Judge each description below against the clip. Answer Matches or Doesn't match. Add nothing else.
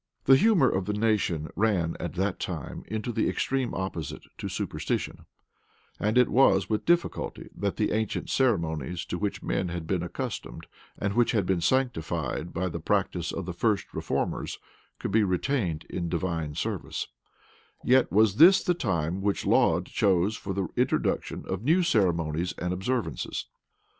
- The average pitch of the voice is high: Doesn't match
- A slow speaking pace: Doesn't match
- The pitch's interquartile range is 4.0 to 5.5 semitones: Matches